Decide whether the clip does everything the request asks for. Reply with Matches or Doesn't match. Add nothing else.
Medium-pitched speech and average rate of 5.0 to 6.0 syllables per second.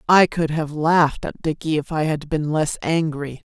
Doesn't match